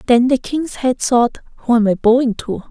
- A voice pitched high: Yes, high, 245 Hz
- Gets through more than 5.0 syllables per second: No, 4.9 syllables/s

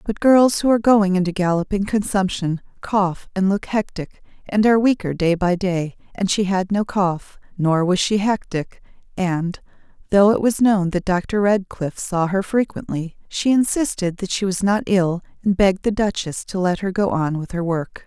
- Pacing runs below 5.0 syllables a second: Yes, 4.6 syllables/s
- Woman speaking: Yes, female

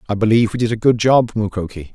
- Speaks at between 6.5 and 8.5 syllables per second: Yes, 6.8 syllables/s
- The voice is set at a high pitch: No, low, 110 Hz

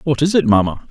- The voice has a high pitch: No, low, 135 Hz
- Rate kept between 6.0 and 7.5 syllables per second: Yes, 6.3 syllables/s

